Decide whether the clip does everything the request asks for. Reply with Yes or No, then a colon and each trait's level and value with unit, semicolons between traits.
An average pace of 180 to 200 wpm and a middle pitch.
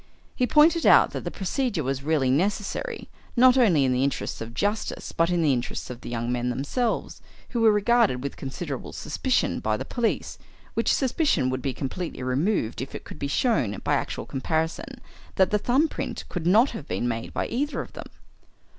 Yes: average, 195 wpm; medium, 165 Hz